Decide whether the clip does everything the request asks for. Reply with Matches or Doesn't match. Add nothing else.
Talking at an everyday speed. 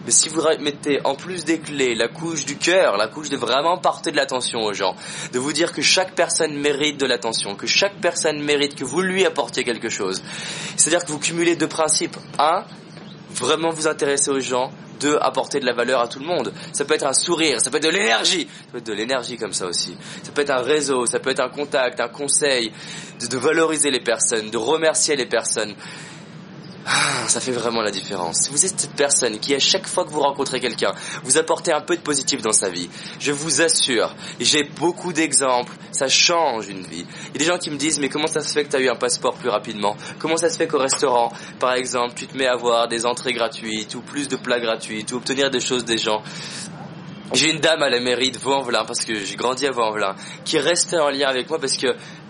Doesn't match